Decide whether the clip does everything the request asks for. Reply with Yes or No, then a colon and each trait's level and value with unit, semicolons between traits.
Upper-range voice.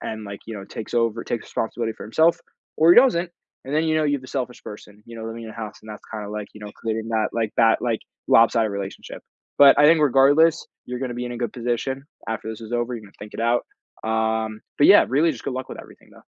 No: low, 115 Hz